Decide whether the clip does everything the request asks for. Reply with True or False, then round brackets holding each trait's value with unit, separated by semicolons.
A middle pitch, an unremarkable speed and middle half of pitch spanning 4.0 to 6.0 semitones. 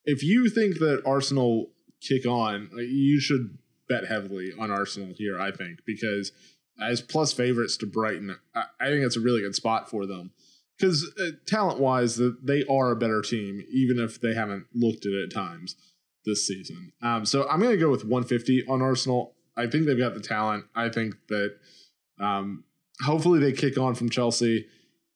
False (120 Hz; 185 wpm; 4.5 semitones)